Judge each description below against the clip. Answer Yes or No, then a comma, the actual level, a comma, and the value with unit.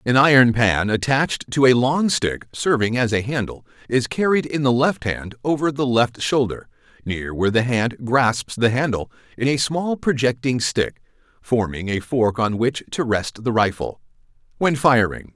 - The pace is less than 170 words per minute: No, average, 175 wpm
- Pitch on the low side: Yes, low, 125 Hz